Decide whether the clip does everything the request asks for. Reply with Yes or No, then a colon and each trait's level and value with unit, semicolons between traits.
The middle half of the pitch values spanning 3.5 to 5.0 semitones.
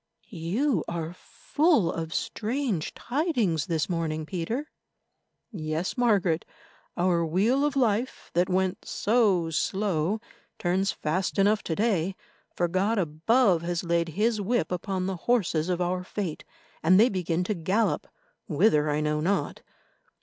Yes: average, 4.6 semitones